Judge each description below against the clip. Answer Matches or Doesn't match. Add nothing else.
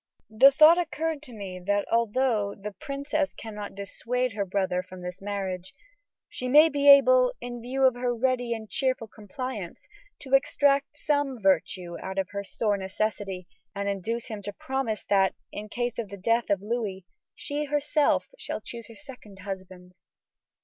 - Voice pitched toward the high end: Matches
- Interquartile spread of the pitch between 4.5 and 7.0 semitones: Matches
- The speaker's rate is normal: Matches